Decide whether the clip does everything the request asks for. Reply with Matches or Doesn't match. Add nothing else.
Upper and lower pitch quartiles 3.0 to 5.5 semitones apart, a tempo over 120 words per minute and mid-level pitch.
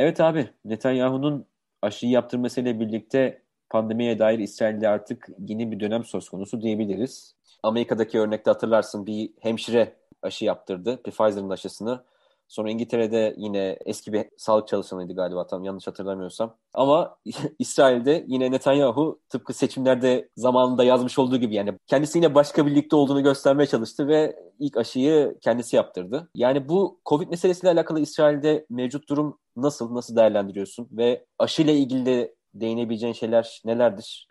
Doesn't match